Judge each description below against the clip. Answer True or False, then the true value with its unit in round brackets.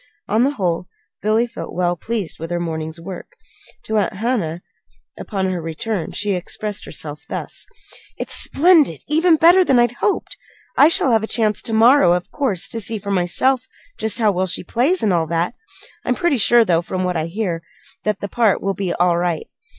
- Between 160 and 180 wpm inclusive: False (195 wpm)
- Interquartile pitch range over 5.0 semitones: True (5.4 semitones)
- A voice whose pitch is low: False (205 Hz)